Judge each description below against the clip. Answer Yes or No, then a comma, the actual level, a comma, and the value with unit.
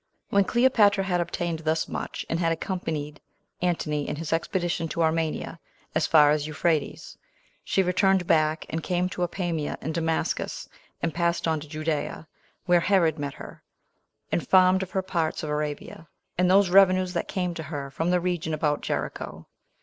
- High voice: No, medium, 165 Hz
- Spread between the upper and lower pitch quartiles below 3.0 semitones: Yes, narrow, 2.5 semitones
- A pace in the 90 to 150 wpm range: No, average, 170 wpm